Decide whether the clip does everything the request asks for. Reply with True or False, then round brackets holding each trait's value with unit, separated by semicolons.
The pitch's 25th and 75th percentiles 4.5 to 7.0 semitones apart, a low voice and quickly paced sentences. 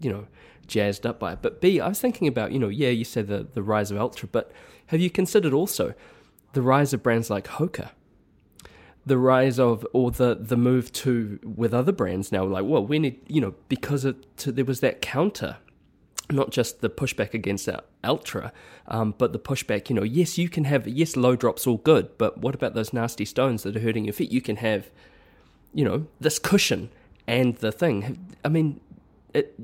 True (4.9 semitones; 125 Hz; 210 wpm)